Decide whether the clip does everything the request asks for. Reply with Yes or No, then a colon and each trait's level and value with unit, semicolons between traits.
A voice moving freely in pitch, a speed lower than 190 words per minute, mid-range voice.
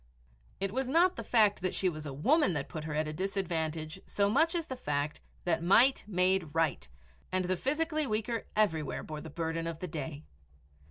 No: wide, 6.0 semitones; average, 200 wpm; medium, 180 Hz